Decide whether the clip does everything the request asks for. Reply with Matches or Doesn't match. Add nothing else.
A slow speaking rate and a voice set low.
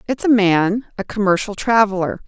Doesn't match